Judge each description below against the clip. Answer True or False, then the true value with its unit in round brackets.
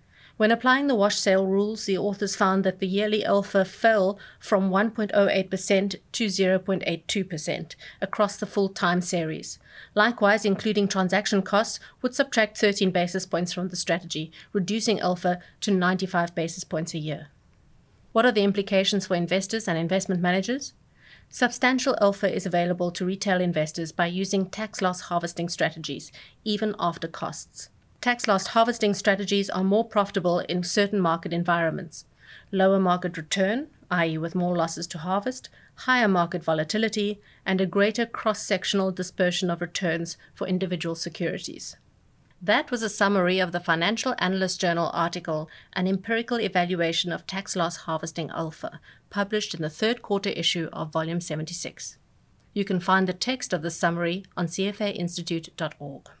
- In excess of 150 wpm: False (145 wpm)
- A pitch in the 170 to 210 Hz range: True (190 Hz)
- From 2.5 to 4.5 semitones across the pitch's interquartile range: True (3.0 semitones)